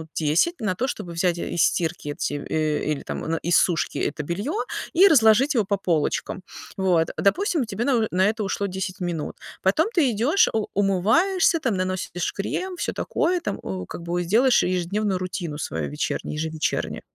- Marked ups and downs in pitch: Yes, wide, 5.7 semitones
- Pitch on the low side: No, high, 190 Hz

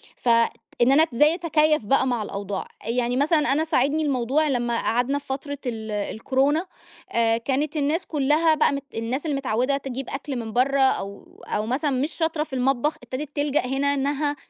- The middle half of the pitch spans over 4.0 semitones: No, average, 3.7 semitones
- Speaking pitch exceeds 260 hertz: Yes, very high, 270 Hz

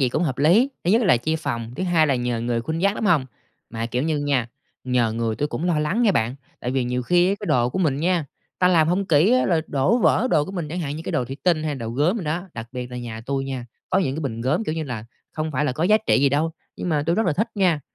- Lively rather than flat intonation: Yes, wide, 5.8 semitones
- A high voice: No, medium, 150 Hz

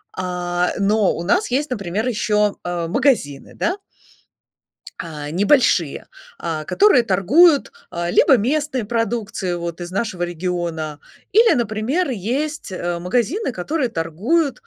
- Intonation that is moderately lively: No, wide, 7.0 semitones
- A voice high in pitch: Yes, high, 205 Hz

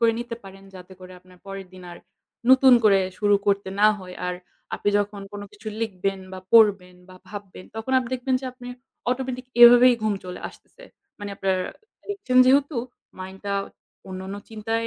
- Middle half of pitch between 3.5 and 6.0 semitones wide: Yes, average, 4.4 semitones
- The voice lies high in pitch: Yes, high, 205 Hz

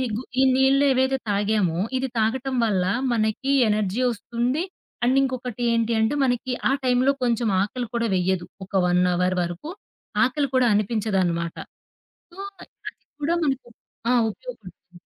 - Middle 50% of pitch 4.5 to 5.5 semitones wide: Yes, average, 4.8 semitones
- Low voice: No, high, 235 Hz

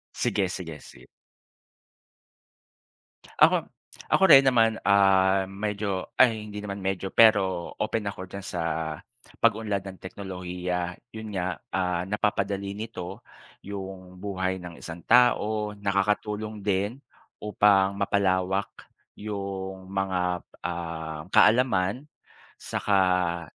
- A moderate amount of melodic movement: No, narrow, 2.2 semitones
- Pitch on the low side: Yes, very low, 95 Hz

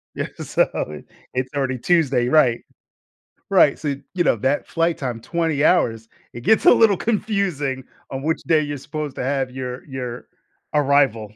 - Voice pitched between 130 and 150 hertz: Yes, medium, 140 Hz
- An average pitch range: Yes, average, 4.2 semitones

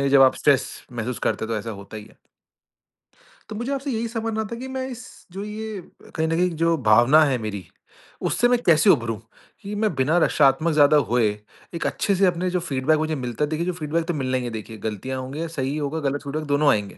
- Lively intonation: Yes, wide, 5.9 semitones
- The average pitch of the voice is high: No, medium, 150 Hz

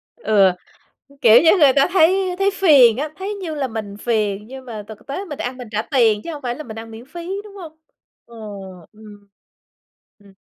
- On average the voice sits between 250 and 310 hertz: Yes, very high, 260 Hz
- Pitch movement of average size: No, wide, 7.2 semitones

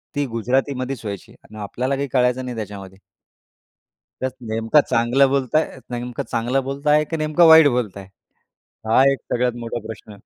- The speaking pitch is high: No, low, 125 Hz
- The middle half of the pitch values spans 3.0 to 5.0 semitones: Yes, average, 3.4 semitones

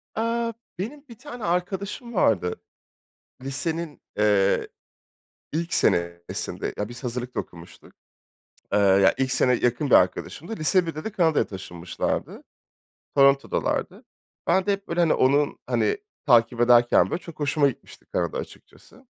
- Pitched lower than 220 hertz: Yes, medium, 140 Hz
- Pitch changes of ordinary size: No, wide, 7.6 semitones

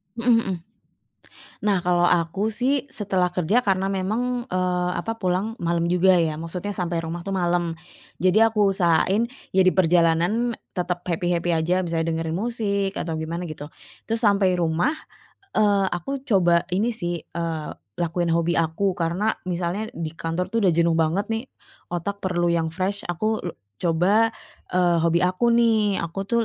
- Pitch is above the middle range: No, medium, 180 Hz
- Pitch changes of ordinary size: Yes, average, 3.2 semitones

